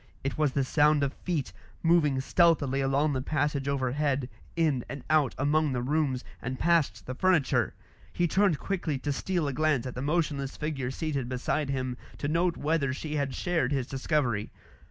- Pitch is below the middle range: No, medium, 145 Hz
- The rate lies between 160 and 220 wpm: Yes, average, 175 wpm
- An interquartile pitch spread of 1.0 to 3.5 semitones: Yes, average, 2.9 semitones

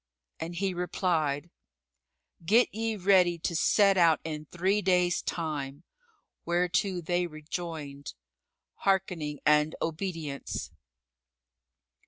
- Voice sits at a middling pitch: Yes, medium, 175 Hz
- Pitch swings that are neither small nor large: Yes, average, 3.3 semitones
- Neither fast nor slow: No, slow, 95 wpm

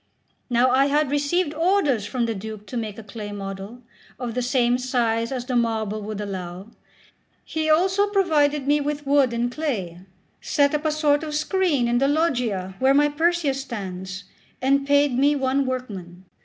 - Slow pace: No, average, 175 wpm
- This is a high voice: Yes, very high, 255 Hz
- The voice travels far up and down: No, average, 5.0 semitones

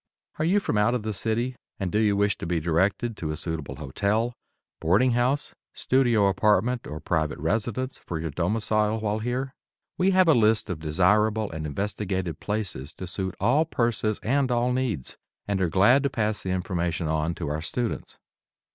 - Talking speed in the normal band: Yes, average, 180 wpm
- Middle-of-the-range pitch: No, low, 105 Hz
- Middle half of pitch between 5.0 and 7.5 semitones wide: Yes, wide, 5.5 semitones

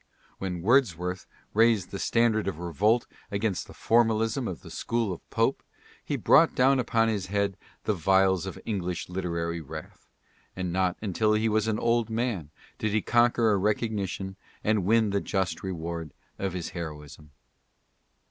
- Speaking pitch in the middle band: No, low, 100 Hz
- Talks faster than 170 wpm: No, average, 155 wpm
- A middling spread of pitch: Yes, average, 3.8 semitones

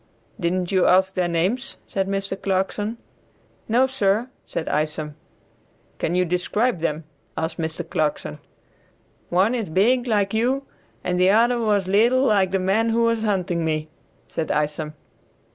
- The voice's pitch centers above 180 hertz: Yes, high, 190 Hz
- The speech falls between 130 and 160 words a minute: Yes, average, 145 wpm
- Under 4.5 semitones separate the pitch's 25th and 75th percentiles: No, average, 4.8 semitones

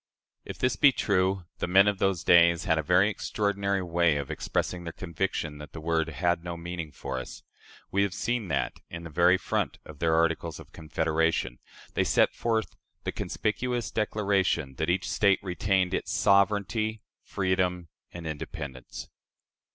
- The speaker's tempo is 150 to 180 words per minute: Yes, average, 165 wpm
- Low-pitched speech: Yes, very low, 90 Hz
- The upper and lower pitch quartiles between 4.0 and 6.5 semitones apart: No, average, 3.4 semitones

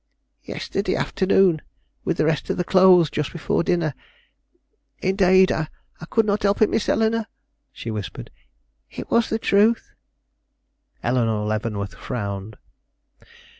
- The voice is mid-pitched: Yes, medium, 175 Hz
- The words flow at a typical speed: No, slow, 125 wpm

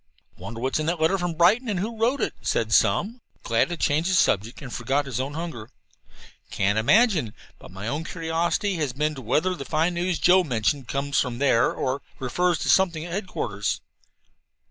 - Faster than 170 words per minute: Yes, average, 195 wpm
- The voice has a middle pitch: Yes, medium, 155 Hz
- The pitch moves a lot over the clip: Yes, wide, 5.8 semitones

